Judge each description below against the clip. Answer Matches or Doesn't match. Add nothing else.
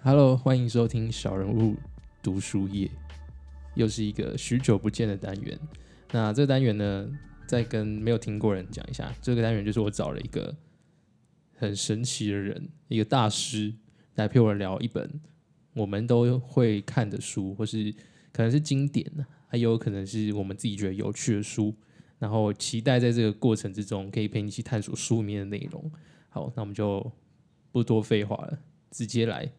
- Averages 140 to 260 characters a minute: Doesn't match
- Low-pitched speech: Matches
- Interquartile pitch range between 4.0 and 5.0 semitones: Matches